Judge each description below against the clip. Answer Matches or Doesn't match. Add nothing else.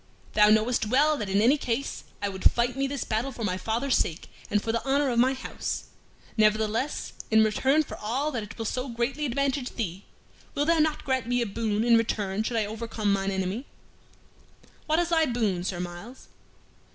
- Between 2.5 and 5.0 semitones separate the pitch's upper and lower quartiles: Matches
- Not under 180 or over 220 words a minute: Matches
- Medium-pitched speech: Doesn't match